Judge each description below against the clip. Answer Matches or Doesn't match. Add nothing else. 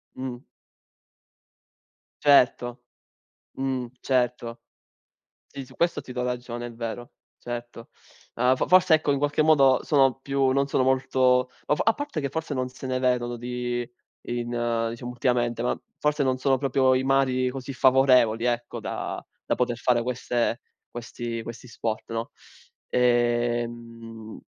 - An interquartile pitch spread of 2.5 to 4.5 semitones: Doesn't match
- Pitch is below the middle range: Matches